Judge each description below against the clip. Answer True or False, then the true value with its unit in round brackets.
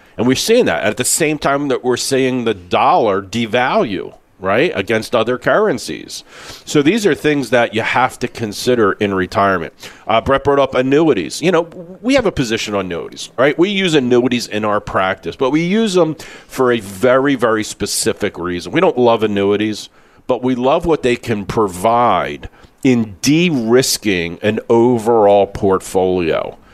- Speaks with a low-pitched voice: True (125 Hz)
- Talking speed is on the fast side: False (170 wpm)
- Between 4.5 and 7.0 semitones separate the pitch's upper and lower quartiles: True (4.9 semitones)